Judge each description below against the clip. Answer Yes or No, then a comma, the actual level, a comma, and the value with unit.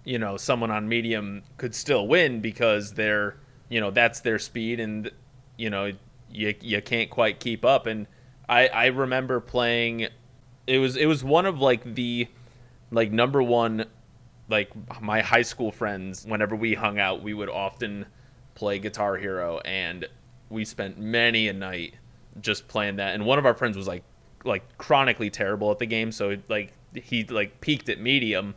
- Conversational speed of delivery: Yes, average, 180 wpm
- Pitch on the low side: Yes, low, 115 Hz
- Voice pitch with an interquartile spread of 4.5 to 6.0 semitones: No, average, 2.8 semitones